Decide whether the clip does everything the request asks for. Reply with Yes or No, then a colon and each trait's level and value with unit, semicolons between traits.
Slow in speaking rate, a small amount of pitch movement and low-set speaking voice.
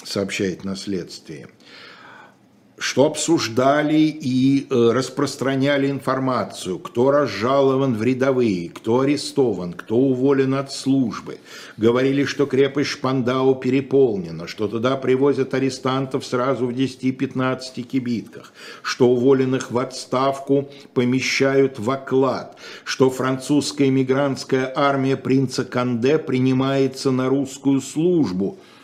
Yes: slow, 100 wpm; narrow, 1.3 semitones; low, 130 Hz